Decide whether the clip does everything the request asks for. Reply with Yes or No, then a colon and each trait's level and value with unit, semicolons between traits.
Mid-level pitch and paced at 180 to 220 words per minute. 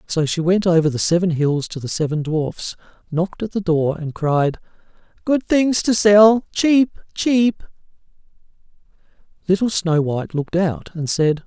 No: medium, 175 Hz; average, 155 wpm